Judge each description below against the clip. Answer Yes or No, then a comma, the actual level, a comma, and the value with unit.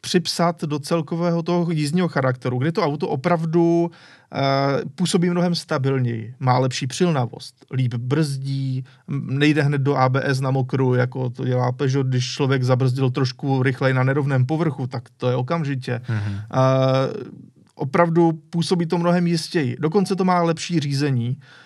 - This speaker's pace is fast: No, average, 145 wpm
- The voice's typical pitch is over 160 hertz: No, medium, 140 Hz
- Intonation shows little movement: No, average, 4.4 semitones